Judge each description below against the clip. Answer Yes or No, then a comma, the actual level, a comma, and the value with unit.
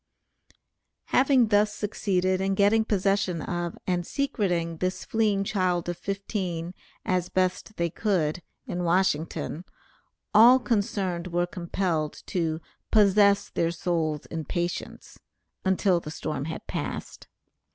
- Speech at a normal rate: No, slow, 120 wpm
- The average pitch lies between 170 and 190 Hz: Yes, medium, 185 Hz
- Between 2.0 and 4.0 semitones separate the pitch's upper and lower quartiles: Yes, average, 2.9 semitones